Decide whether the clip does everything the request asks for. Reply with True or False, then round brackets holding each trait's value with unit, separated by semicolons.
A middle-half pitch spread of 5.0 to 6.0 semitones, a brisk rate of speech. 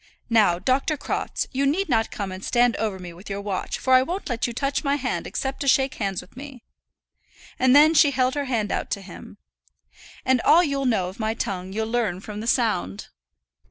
True (5.3 semitones; 215 wpm)